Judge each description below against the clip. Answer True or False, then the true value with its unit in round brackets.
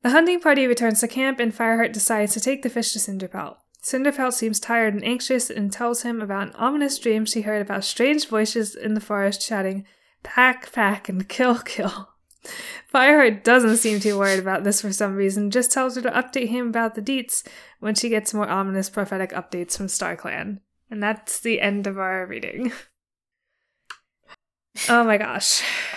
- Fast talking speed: False (185 wpm)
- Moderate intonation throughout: True (3.6 semitones)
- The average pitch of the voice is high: True (225 Hz)